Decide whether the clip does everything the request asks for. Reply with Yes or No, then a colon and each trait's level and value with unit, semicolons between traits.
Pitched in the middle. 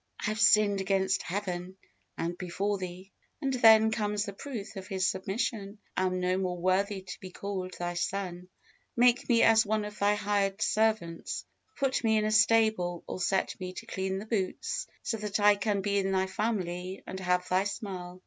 No: high, 195 Hz